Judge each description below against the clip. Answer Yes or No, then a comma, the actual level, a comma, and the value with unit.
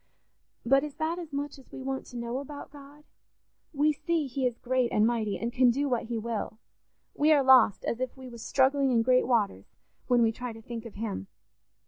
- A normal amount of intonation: Yes, average, 3.2 semitones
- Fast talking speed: Yes, fast, 215 wpm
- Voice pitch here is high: Yes, very high, 255 Hz